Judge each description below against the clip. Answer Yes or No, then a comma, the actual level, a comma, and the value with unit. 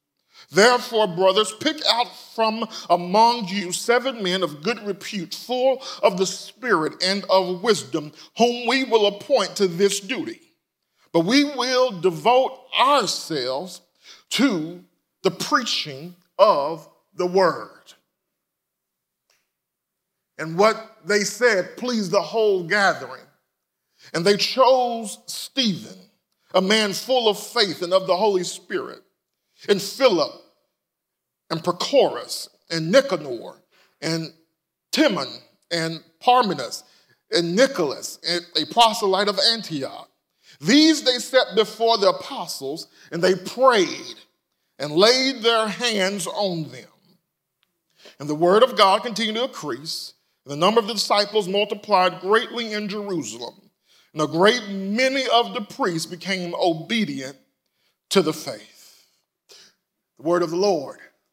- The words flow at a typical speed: No, slow, 125 wpm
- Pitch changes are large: No, average, 4.7 semitones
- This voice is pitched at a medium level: No, high, 200 Hz